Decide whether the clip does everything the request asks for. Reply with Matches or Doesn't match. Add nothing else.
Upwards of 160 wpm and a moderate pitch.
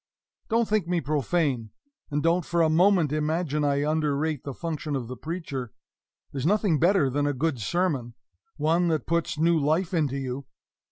Matches